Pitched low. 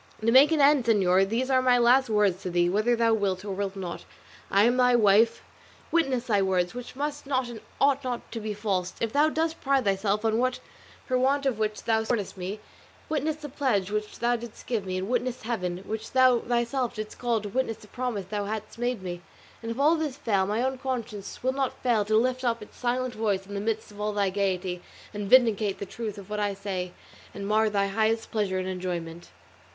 No: high, 220 Hz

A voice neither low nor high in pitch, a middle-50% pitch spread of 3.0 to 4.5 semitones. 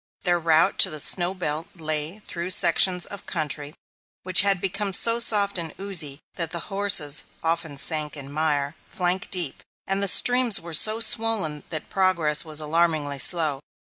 Yes: medium, 170 Hz; average, 4.1 semitones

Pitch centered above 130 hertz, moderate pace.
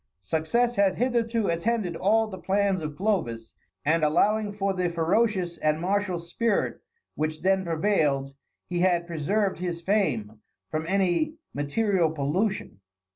No: medium, 185 Hz; slow, 130 wpm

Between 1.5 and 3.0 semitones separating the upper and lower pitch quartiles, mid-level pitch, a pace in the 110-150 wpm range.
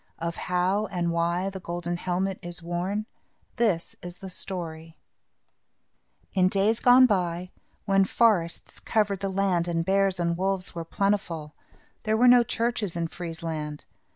Yes: narrow, 2.6 semitones; medium, 180 Hz; average, 145 wpm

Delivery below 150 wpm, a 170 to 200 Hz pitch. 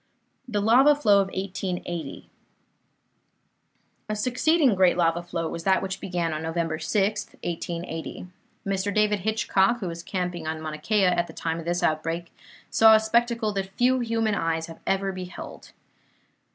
No: average, 155 wpm; high, 190 Hz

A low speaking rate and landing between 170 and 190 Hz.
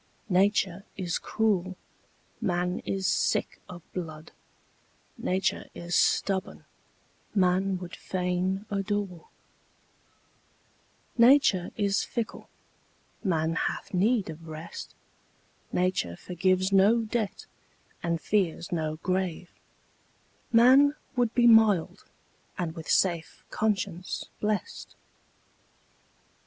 Yes: slow, 90 wpm; medium, 185 Hz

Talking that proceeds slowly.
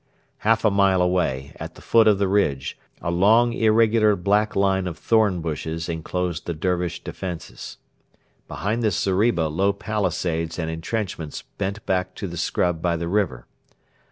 No: average, 155 wpm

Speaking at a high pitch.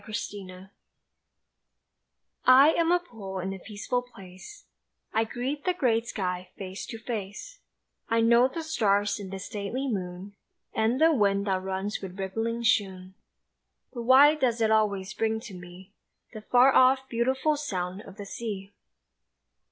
Yes: high, 220 Hz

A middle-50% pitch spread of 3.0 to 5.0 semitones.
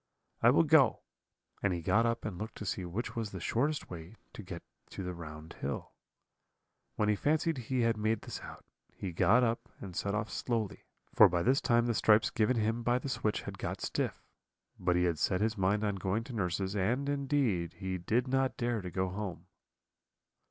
Yes: average, 4.3 semitones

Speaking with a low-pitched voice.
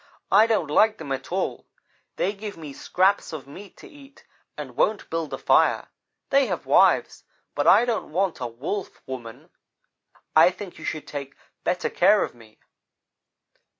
No: medium, 180 Hz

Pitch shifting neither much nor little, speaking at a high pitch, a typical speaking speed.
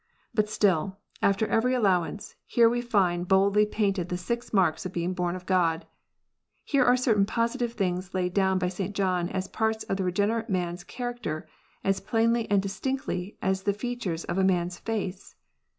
Yes: average, 3.7 semitones; high, 195 Hz; average, 180 wpm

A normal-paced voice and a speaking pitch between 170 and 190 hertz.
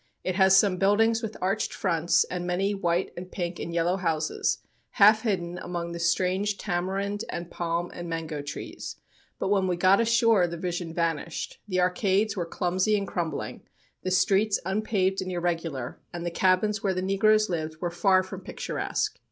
Yes: average, 175 wpm; medium, 185 Hz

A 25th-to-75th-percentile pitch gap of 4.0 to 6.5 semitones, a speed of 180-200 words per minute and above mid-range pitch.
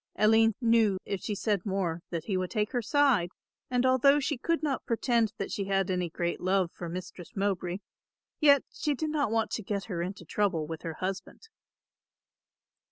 Yes: average, 4.9 semitones; average, 185 wpm; high, 200 Hz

